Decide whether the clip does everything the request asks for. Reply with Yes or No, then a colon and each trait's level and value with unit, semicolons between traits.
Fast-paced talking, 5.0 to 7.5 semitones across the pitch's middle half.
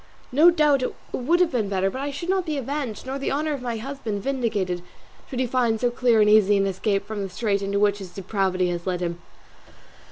Yes: fast, 230 wpm; wide, 5.6 semitones